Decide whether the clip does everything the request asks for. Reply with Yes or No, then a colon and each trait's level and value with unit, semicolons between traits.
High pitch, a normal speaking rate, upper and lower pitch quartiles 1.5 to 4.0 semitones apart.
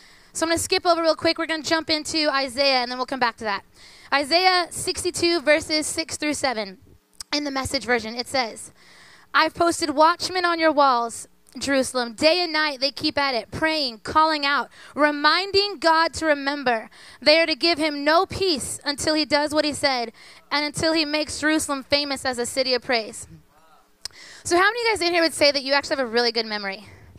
No: very high, 300 Hz; fast, 210 wpm; average, 3.5 semitones